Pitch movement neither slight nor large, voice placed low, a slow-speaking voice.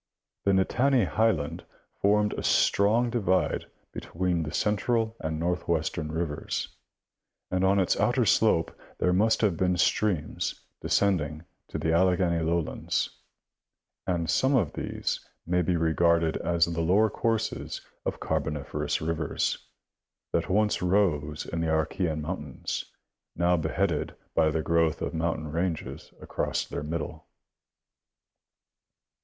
Yes: average, 3.5 semitones; very low, 85 Hz; slow, 125 wpm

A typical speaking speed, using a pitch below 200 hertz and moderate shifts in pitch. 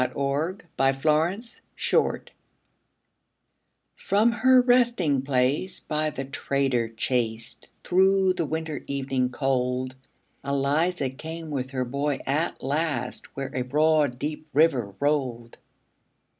No: slow, 110 wpm; medium, 140 Hz; average, 3.7 semitones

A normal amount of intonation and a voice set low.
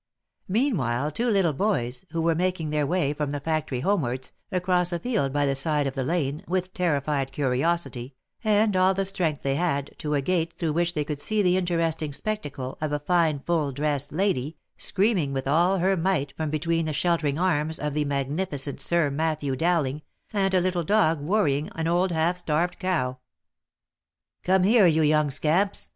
No: average, 4.1 semitones; medium, 160 Hz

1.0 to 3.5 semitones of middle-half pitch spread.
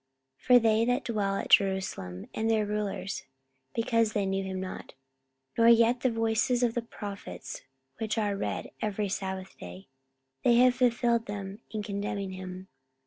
Yes: average, 3.0 semitones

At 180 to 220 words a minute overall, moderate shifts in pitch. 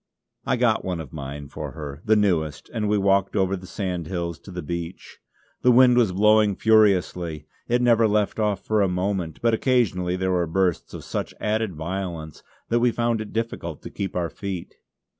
Yes: average, 190 wpm; average, 4.0 semitones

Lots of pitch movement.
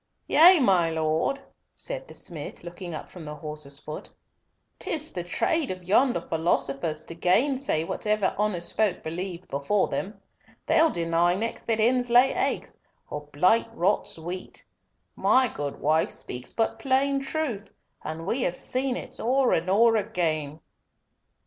Yes: wide, 7.2 semitones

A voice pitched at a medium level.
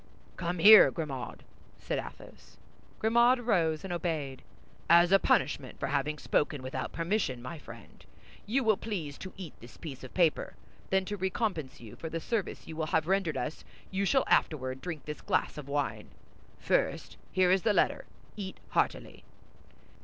Yes: medium, 170 Hz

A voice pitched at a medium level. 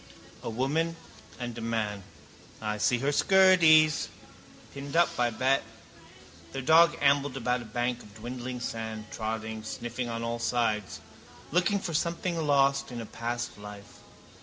No: low, 125 Hz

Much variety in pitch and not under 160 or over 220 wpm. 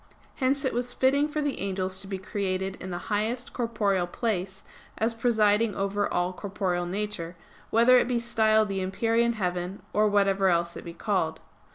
No: average, 3.6 semitones; average, 175 wpm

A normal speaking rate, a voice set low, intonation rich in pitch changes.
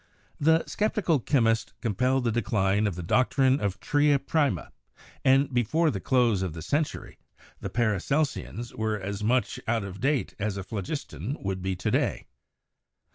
Yes: average, 160 wpm; low, 120 Hz; wide, 5.8 semitones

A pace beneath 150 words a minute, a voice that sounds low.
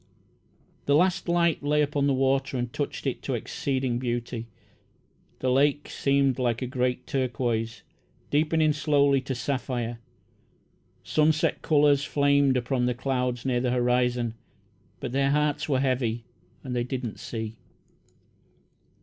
Yes: slow, 135 wpm; low, 130 Hz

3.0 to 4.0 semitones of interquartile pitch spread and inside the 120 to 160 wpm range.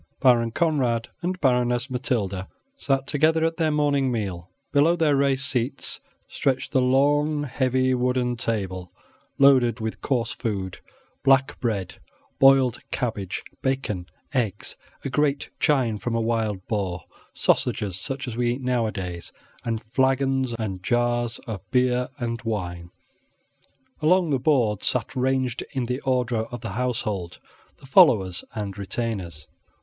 Yes: average, 3.6 semitones; slow, 135 wpm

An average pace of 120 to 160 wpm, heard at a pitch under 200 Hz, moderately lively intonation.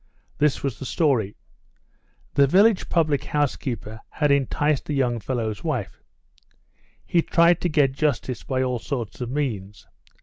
Yes: average, 145 wpm; low, 135 Hz; average, 3.9 semitones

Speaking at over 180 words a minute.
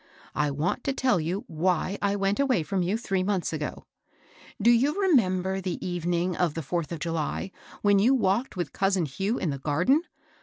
Yes: average, 190 wpm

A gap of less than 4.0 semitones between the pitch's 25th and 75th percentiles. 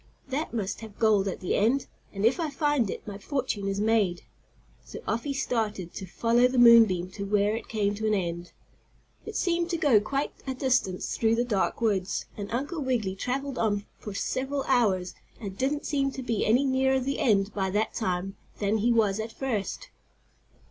No: average, 4.7 semitones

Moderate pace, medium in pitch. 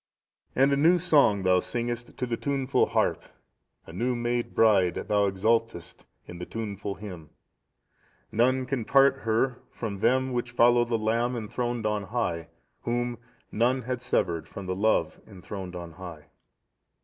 No: average, 150 wpm; low, 115 Hz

